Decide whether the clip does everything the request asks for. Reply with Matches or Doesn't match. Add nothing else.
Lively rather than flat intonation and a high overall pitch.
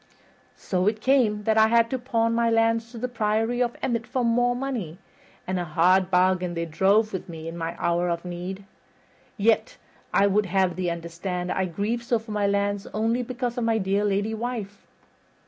Doesn't match